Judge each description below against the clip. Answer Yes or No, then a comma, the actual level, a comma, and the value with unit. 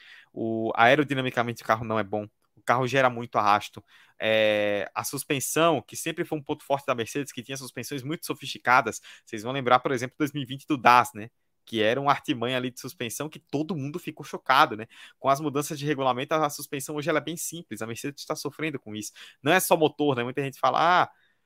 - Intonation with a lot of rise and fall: No, average, 4.2 semitones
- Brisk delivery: Yes, fast, 215 wpm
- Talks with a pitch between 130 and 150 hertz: Yes, low, 135 Hz